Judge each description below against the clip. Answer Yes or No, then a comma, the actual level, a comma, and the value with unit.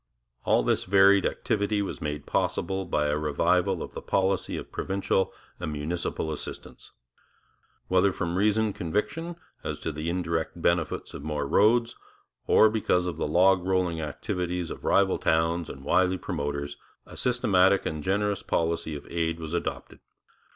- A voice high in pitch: No, very low, 90 Hz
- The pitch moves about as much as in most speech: Yes, average, 3.4 semitones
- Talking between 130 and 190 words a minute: Yes, average, 150 wpm